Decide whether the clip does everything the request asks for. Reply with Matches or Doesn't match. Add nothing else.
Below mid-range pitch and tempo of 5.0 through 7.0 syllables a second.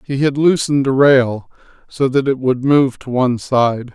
Doesn't match